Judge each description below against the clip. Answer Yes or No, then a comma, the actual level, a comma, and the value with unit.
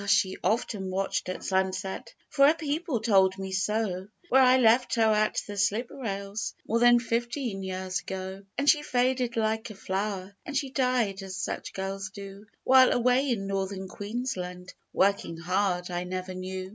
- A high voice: Yes, high, 200 Hz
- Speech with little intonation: No, average, 4.2 semitones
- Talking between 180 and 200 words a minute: No, average, 170 wpm